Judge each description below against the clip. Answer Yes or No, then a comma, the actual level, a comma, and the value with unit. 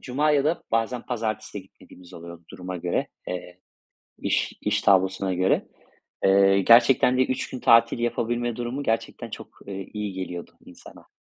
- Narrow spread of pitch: No, average, 4.5 semitones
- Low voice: Yes, low, 110 Hz